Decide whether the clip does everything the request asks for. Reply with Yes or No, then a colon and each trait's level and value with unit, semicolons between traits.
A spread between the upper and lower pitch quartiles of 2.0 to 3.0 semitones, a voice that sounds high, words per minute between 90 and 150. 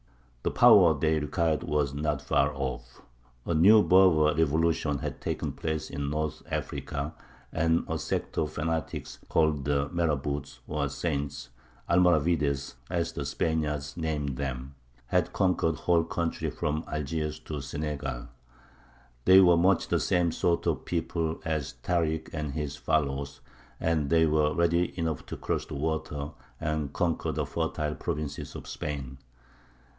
No: narrow, 2.5 semitones; very low, 75 Hz; average, 145 wpm